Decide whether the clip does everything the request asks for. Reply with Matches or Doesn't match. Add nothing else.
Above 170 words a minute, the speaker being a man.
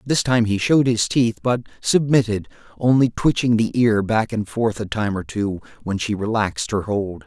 Matches